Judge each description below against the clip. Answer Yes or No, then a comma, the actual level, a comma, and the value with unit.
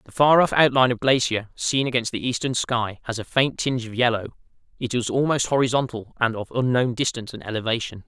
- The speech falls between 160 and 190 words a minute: No, average, 200 wpm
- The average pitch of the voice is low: Yes, low, 120 Hz